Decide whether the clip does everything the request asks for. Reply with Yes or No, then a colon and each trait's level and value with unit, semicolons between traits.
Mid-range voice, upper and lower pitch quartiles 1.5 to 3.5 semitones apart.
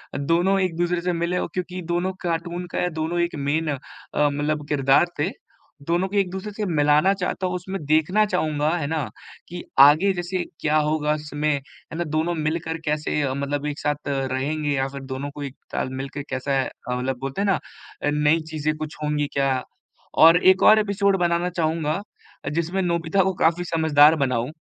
Yes: medium, 160 Hz; average, 3.2 semitones